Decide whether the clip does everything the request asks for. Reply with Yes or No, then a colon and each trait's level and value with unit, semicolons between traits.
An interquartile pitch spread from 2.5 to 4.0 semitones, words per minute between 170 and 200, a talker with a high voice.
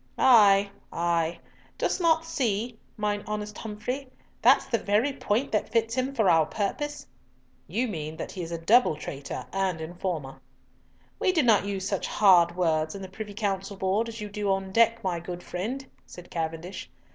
No: average, 4.5 semitones; average, 175 wpm; high, 200 Hz